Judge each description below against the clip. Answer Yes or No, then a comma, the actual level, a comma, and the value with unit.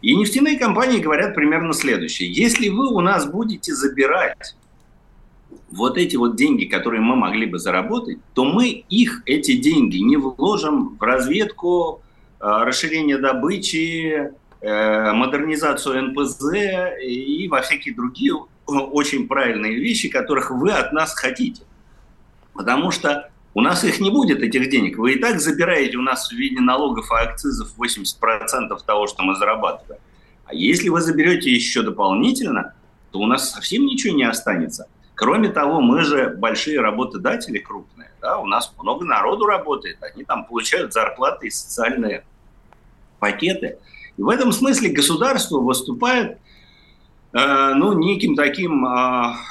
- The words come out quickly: No, average, 140 wpm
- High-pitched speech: Yes, high, 195 Hz